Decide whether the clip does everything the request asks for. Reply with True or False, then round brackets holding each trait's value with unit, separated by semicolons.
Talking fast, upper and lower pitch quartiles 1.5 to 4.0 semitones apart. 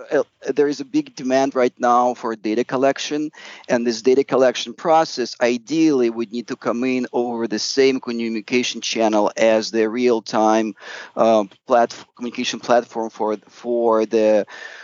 False (150 wpm; 2.5 semitones)